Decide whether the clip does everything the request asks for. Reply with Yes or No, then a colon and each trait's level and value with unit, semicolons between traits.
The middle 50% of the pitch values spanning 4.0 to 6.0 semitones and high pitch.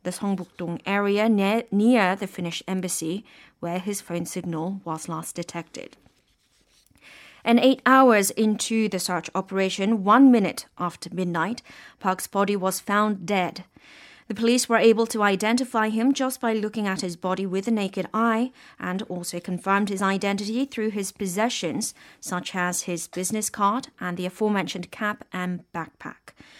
No: average, 3.6 semitones; high, 200 Hz